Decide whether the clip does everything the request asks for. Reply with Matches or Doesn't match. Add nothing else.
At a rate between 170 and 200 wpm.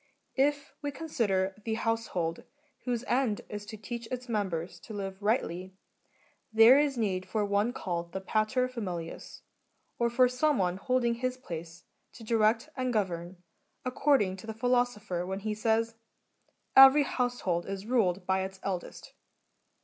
Doesn't match